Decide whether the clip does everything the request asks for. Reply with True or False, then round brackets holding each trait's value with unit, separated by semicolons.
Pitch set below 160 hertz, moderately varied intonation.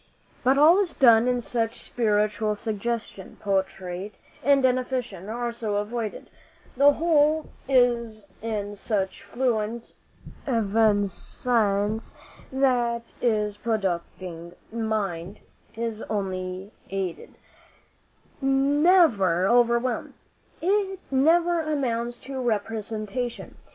False (230 Hz; 3.9 semitones)